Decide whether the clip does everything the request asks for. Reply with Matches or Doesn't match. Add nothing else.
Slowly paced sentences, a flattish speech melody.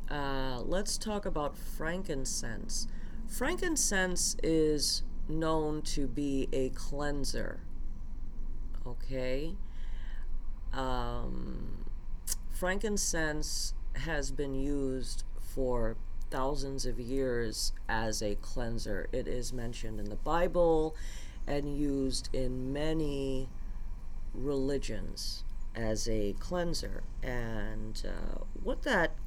Doesn't match